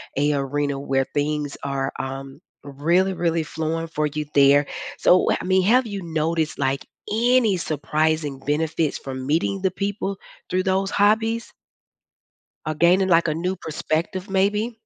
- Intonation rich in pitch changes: No, average, 4.6 semitones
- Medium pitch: Yes, medium, 160 Hz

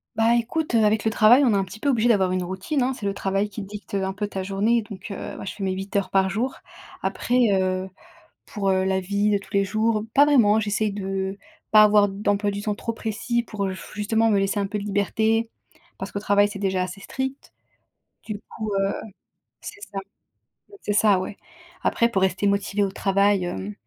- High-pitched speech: Yes, high, 205 Hz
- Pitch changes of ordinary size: No, narrow, 2.2 semitones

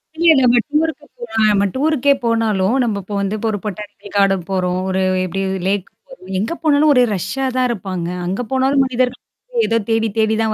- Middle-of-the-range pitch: No, high, 225 Hz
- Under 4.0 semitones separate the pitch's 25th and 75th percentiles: No, average, 5.0 semitones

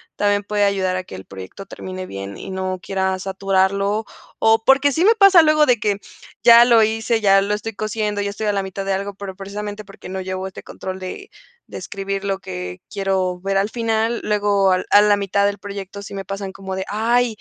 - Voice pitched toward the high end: Yes, high, 200 Hz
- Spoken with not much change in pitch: Yes, narrow, 2.0 semitones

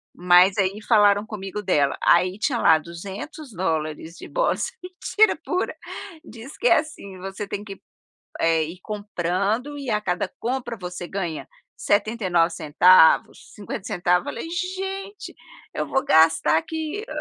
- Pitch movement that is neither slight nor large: No, wide, 7.1 semitones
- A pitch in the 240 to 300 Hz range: No, high, 200 Hz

